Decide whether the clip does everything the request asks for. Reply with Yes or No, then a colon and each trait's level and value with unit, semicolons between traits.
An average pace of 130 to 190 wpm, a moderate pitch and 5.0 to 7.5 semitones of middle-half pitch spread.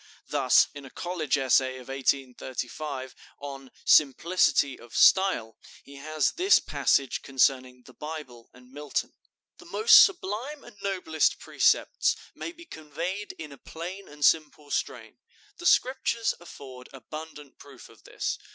Yes: slow, 135 wpm; medium, 145 Hz; average, 5.3 semitones